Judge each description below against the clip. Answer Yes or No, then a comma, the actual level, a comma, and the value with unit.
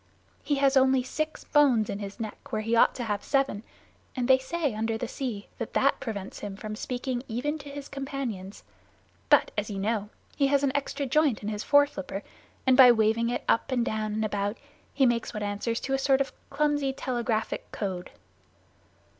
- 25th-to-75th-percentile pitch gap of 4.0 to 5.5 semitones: Yes, average, 4.4 semitones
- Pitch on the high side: Yes, high, 240 Hz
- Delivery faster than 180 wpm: Yes, average, 195 wpm